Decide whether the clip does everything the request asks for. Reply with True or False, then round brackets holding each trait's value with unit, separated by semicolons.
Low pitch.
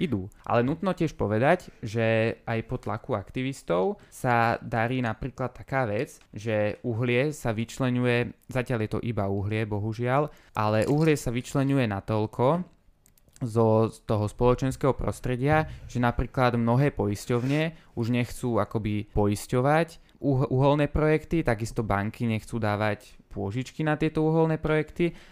True (120 Hz)